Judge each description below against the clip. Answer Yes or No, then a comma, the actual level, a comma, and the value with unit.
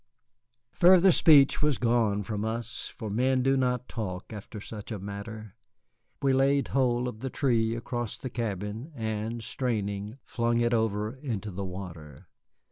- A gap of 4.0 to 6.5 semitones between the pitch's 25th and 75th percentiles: No, average, 3.5 semitones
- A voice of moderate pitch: No, low, 115 Hz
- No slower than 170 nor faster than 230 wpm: No, average, 150 wpm